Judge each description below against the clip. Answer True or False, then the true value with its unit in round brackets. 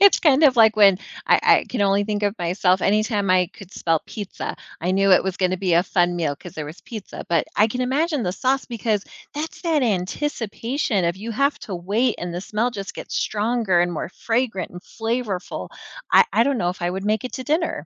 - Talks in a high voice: True (205 Hz)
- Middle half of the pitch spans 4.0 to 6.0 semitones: True (5.2 semitones)